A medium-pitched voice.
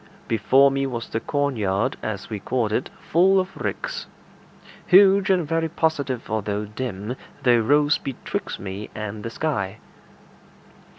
No: low, 125 Hz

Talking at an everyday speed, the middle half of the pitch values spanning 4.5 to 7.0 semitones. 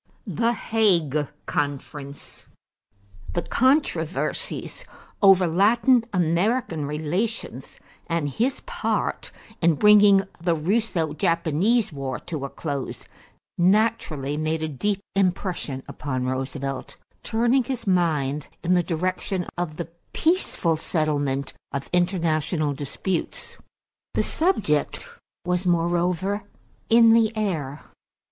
No: slow, 100 wpm; wide, 5.5 semitones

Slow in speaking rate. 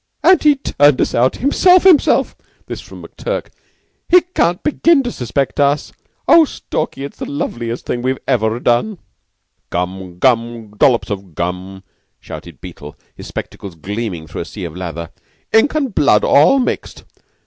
No: average, 160 wpm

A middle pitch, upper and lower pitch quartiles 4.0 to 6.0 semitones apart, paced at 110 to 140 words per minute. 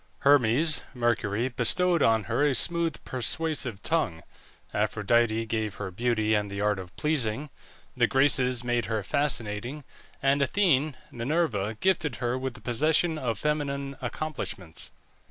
No: low, 125 Hz; average, 5.2 semitones; slow, 135 wpm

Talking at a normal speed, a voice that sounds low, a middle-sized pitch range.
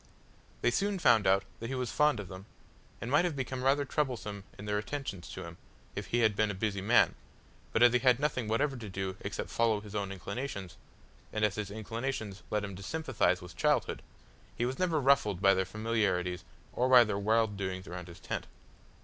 No: fast, 210 wpm; low, 110 Hz; average, 4.6 semitones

